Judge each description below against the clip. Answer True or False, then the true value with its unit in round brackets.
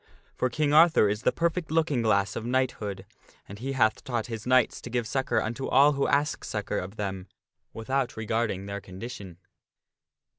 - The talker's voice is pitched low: True (120 Hz)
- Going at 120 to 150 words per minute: False (175 wpm)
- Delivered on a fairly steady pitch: False (4.6 semitones)